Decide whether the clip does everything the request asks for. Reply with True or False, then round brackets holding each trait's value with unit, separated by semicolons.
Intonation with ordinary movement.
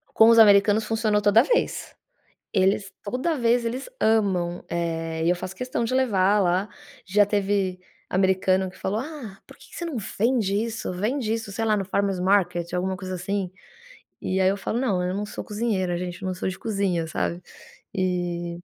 True (3.3 semitones)